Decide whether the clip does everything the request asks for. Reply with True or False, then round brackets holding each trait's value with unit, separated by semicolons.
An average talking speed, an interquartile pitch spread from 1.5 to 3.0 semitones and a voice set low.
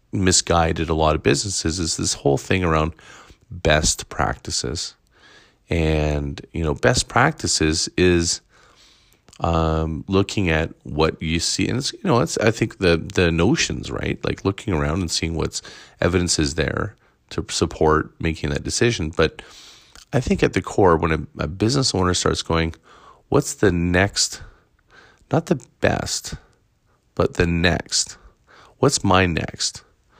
True (145 wpm; 2.7 semitones; 85 Hz)